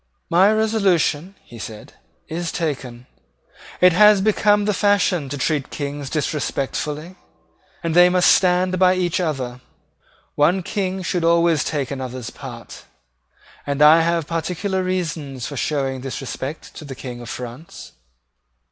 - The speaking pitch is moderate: Yes, medium, 165 Hz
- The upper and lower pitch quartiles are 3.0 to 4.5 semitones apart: No, average, 4.9 semitones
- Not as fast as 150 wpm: Yes, average, 140 wpm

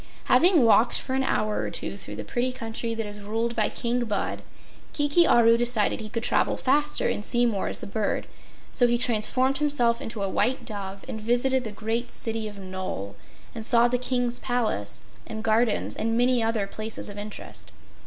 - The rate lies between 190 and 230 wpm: Yes, average, 195 wpm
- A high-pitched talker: Yes, high, 230 Hz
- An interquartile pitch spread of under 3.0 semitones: Yes, narrow, 2.4 semitones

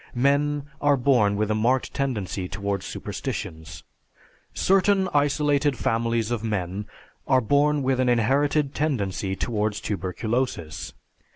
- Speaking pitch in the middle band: No, low, 120 Hz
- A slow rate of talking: Yes, slow, 115 wpm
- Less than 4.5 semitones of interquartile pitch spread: No, wide, 5.6 semitones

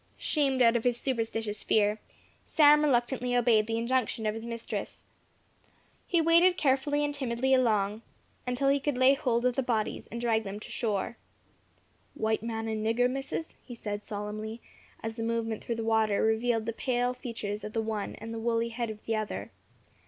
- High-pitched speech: Yes, high, 230 Hz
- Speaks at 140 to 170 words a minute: No, average, 180 wpm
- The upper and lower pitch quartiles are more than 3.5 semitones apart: No, narrow, 2.5 semitones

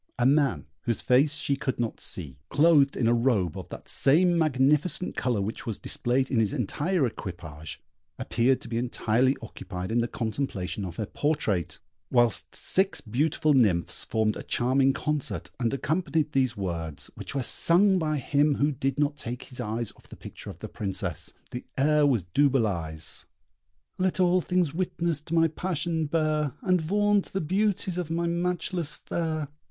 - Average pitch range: No, wide, 5.9 semitones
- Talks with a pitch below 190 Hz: Yes, low, 135 Hz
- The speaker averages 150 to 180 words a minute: Yes, average, 170 wpm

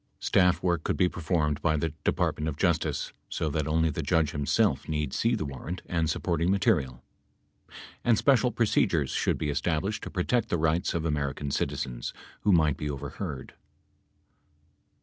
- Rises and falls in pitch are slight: No, average, 3.5 semitones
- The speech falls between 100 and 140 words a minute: No, average, 165 wpm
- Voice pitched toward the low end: Yes, very low, 80 Hz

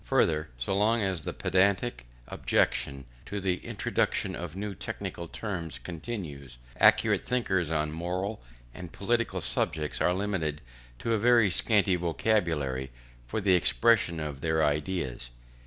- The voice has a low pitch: Yes, very low, 90 Hz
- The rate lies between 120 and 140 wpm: Yes, slow, 135 wpm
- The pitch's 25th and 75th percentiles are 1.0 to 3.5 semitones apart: No, average, 4.8 semitones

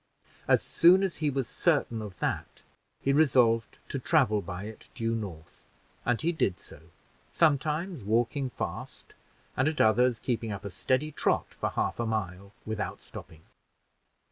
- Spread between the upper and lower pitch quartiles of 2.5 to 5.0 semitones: No, wide, 5.4 semitones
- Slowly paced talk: No, average, 160 wpm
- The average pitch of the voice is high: No, low, 120 Hz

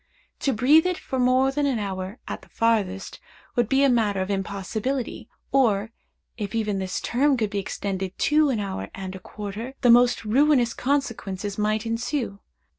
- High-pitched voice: Yes, high, 225 Hz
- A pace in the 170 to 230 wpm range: Yes, average, 175 wpm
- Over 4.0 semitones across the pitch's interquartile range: Yes, average, 4.7 semitones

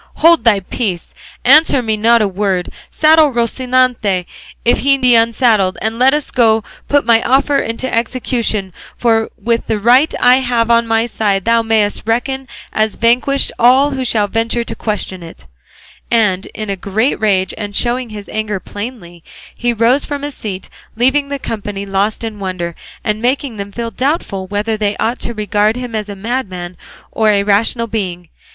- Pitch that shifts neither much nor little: Yes, average, 3.4 semitones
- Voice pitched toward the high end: Yes, high, 225 Hz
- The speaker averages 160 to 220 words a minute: Yes, average, 180 wpm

